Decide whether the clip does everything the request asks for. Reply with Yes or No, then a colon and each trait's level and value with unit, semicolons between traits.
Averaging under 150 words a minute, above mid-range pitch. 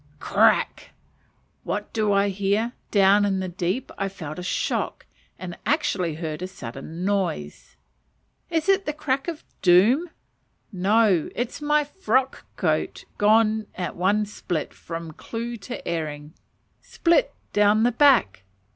Yes: average, 140 wpm; high, 205 Hz